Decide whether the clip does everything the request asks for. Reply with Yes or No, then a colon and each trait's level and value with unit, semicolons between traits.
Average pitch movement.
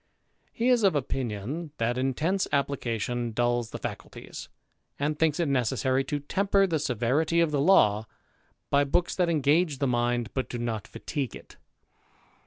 Yes: average, 5.0 semitones